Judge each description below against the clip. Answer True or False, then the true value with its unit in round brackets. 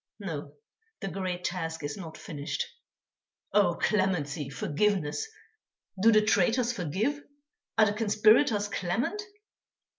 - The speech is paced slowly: True (110 wpm)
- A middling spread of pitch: True (4.8 semitones)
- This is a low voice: False (195 Hz)